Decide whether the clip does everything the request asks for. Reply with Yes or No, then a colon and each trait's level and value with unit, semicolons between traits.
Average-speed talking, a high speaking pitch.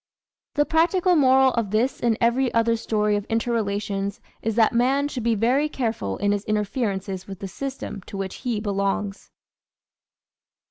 Yes: average, 160 wpm; high, 225 Hz